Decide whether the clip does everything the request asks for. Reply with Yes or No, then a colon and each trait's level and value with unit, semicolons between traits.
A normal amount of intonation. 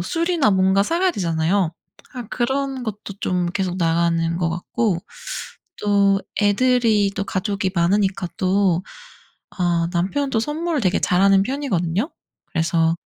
Yes: average, 5.0 semitones